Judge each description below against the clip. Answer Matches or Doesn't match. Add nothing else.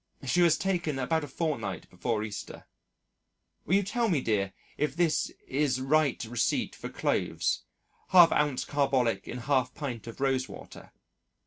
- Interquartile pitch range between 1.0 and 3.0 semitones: Doesn't match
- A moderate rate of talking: Matches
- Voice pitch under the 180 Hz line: Matches